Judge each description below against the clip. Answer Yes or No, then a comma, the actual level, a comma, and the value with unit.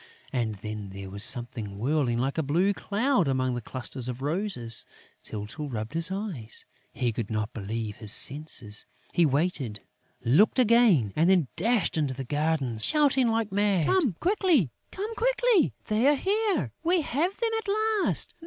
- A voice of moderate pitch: Yes, medium, 155 Hz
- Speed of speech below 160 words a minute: No, average, 165 wpm